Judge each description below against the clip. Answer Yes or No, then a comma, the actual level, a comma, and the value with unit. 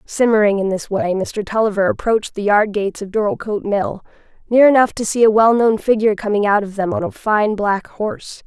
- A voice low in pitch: No, high, 210 Hz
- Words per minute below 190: No, average, 200 wpm